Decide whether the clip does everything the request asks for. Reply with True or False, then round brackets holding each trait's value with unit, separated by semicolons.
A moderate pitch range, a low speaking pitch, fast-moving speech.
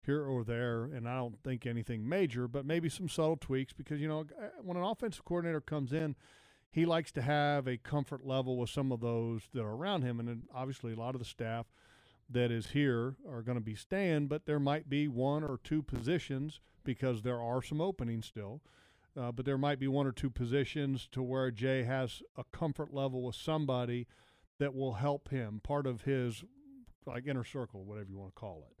True (3.5 semitones; 130 Hz; 210 wpm)